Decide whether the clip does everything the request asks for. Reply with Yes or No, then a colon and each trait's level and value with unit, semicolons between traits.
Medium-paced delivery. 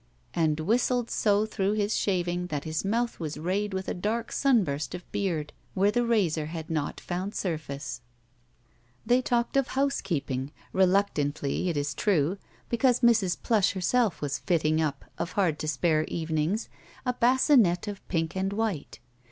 Yes: average, 160 wpm